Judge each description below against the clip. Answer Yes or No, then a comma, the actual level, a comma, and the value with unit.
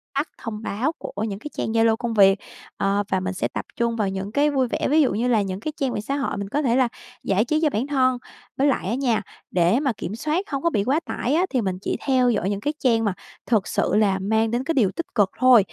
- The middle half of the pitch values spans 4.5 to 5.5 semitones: Yes, average, 5.1 semitones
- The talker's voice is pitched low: No, high, 230 Hz